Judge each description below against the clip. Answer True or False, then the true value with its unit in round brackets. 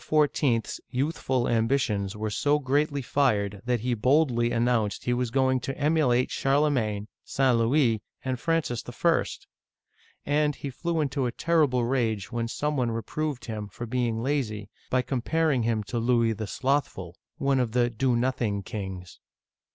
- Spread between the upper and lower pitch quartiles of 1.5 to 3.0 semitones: False (3.6 semitones)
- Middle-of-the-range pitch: False (125 Hz)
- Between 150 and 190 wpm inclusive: True (155 wpm)